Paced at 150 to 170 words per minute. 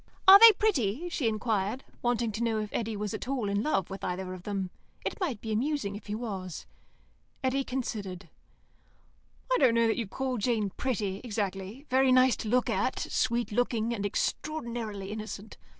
No: average, 180 wpm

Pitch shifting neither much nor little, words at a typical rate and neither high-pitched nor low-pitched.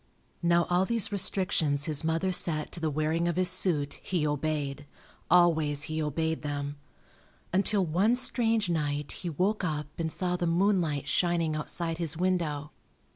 Yes: average, 3.3 semitones; average, 155 wpm; medium, 165 Hz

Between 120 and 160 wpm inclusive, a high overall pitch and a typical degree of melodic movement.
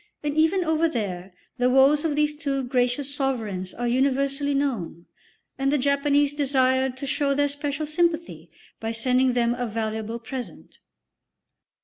Yes: average, 145 wpm; very high, 270 Hz; average, 3.1 semitones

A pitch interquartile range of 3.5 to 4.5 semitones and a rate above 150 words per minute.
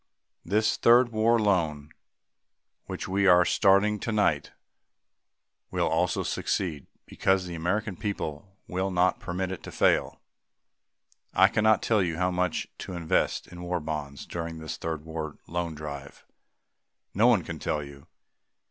No: average, 3.9 semitones; average, 140 wpm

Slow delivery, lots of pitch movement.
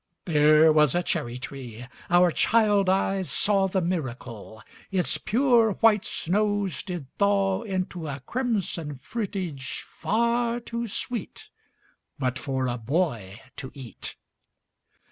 Yes: slow, 120 wpm; wide, 7.1 semitones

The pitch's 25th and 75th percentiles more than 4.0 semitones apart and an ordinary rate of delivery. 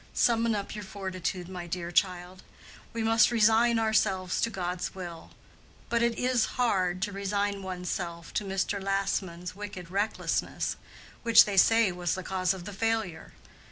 No: average, 3.4 semitones; average, 160 wpm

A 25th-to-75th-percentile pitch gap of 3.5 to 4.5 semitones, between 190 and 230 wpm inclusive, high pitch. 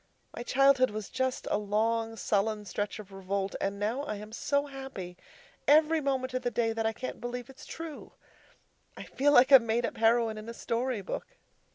Yes: average, 3.8 semitones; average, 195 wpm; high, 230 Hz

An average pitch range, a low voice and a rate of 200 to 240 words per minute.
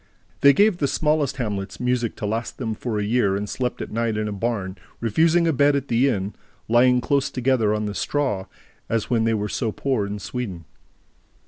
Yes: average, 4.3 semitones; low, 115 Hz; fast, 205 wpm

